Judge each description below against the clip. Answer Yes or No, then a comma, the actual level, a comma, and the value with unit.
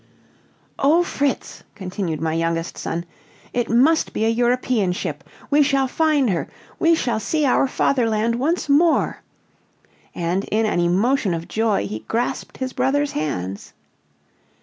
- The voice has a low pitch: No, high, 230 Hz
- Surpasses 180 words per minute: No, average, 140 wpm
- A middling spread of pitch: No, wide, 7.7 semitones